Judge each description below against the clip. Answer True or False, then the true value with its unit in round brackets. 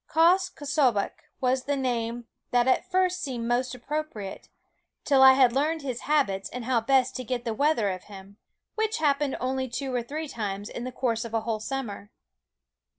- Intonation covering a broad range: False (3.7 semitones)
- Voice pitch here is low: False (255 Hz)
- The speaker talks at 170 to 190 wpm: True (185 wpm)